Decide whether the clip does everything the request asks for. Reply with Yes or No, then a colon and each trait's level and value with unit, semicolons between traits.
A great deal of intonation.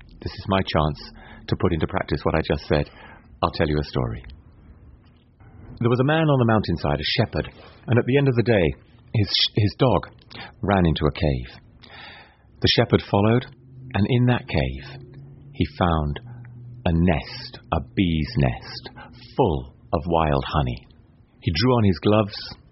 Yes: wide, 6.7 semitones